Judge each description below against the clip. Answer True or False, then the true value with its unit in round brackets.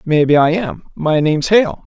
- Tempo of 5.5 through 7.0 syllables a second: False (4.9 syllables/s)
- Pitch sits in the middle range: True (165 Hz)